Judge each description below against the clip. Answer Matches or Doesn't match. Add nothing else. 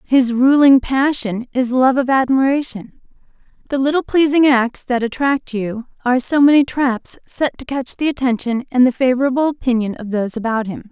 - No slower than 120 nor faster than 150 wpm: Doesn't match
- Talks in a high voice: Matches